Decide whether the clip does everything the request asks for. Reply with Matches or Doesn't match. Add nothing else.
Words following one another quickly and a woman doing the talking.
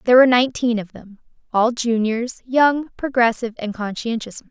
Doesn't match